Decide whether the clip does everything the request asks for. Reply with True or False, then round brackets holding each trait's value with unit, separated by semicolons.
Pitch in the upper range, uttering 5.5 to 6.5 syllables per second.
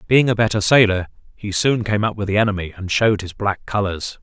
False (105 Hz; 5.8 syllables/s)